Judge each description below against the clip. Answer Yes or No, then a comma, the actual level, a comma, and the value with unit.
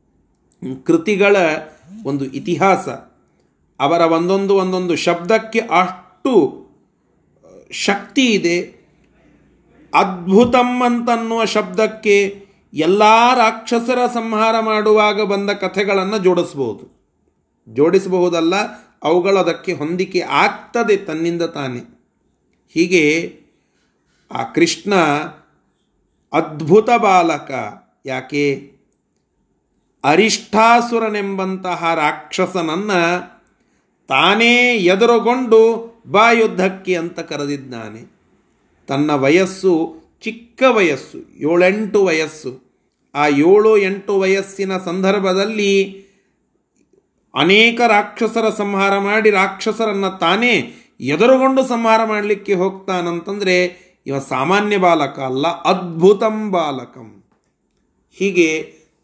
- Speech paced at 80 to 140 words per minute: No, average, 70 wpm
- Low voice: No, high, 190 Hz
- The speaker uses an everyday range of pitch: Yes, average, 4.4 semitones